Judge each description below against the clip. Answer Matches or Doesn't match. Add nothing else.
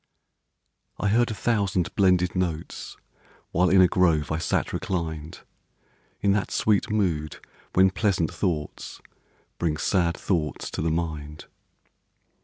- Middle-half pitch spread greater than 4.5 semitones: Doesn't match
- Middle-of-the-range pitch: Doesn't match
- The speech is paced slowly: Matches